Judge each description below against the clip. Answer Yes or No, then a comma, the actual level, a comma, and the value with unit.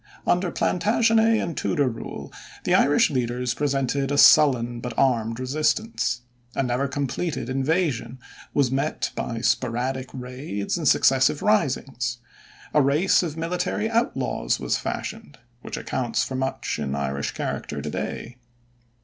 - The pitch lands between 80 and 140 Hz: Yes, low, 135 Hz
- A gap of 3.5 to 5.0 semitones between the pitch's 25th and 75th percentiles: Yes, average, 4.0 semitones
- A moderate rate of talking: No, slow, 130 wpm